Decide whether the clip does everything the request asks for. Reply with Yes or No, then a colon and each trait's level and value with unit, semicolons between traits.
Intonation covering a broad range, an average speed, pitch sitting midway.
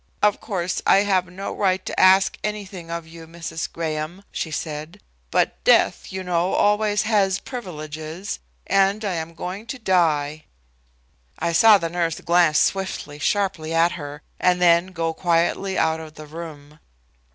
No: average, 3.2 semitones; average, 155 wpm; medium, 175 Hz